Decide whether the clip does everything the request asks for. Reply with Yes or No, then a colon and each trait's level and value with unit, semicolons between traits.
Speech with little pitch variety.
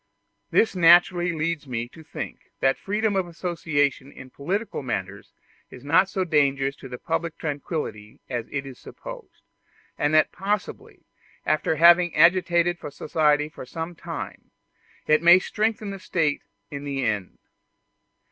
No: average, 3.9 semitones